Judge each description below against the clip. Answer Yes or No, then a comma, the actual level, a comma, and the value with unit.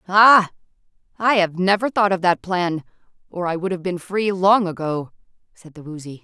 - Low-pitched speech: No, medium, 185 Hz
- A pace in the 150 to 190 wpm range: Yes, average, 185 wpm